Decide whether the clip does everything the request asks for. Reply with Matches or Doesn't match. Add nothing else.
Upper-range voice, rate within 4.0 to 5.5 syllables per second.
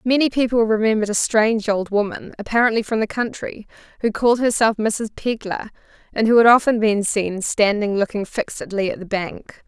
Matches